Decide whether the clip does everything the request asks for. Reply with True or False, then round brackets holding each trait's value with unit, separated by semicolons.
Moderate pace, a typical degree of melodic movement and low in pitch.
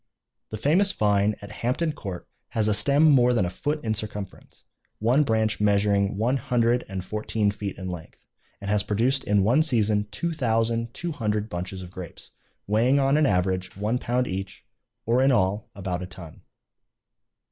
True (175 wpm; 3.9 semitones; 110 Hz)